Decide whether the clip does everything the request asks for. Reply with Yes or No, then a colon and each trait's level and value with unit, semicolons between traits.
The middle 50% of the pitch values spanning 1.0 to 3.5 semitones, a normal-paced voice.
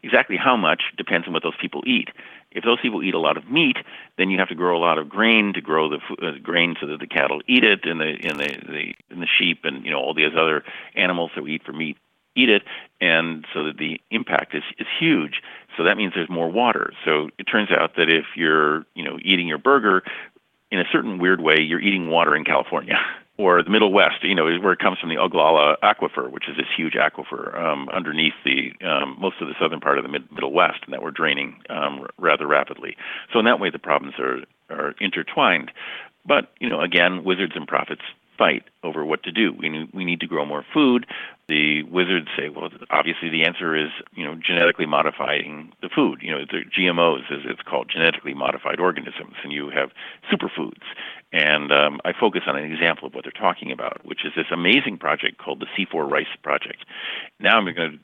No: average, 2.9 semitones; fast, 225 wpm